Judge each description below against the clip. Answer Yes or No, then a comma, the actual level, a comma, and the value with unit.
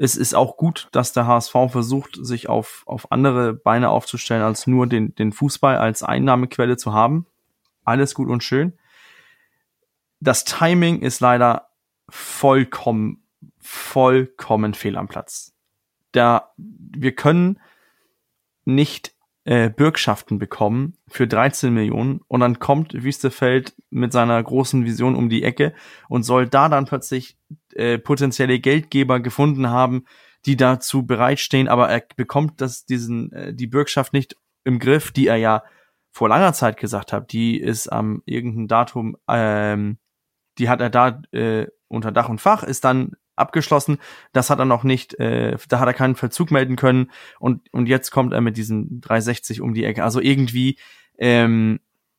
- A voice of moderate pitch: No, low, 125 Hz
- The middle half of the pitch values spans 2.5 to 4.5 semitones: Yes, average, 2.8 semitones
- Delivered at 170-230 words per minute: No, average, 155 wpm